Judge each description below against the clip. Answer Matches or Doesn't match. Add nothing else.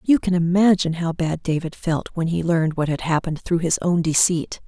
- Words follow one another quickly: Matches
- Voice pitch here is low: Doesn't match